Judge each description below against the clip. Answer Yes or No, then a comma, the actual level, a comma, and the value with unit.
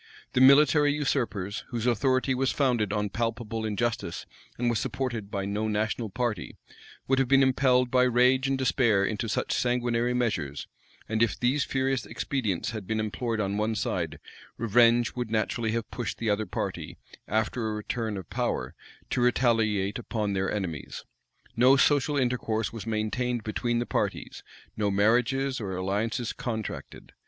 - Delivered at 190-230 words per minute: No, average, 155 wpm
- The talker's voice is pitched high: No, low, 115 Hz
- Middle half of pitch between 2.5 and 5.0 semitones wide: Yes, average, 2.9 semitones